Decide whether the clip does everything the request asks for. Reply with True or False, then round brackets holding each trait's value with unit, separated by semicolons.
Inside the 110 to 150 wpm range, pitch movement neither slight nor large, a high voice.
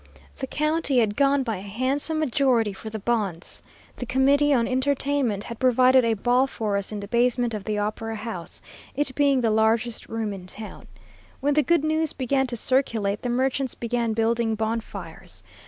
False (180 wpm; 3.6 semitones; 235 Hz)